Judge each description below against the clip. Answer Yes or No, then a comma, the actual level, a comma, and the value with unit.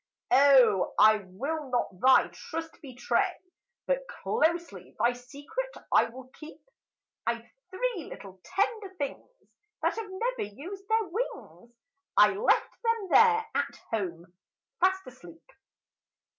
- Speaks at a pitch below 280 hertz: No, very high, 315 Hz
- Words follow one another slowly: Yes, slow, 125 wpm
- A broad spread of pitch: Yes, wide, 9.0 semitones